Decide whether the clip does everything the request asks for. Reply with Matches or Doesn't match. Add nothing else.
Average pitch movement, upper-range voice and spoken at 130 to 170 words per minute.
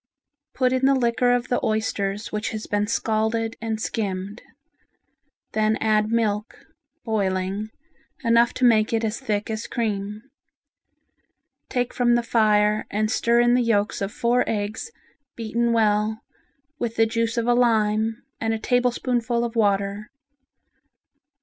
Doesn't match